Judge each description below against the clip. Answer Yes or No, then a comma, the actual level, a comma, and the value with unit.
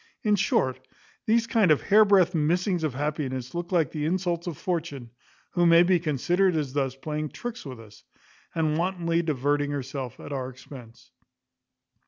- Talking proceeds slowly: No, average, 160 wpm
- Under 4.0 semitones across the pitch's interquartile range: No, average, 4.6 semitones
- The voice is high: No, medium, 155 Hz